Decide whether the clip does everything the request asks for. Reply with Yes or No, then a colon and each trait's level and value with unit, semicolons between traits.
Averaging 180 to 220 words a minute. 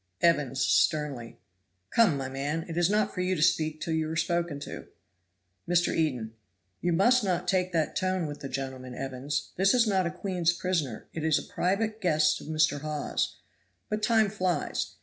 Yes: average, 185 wpm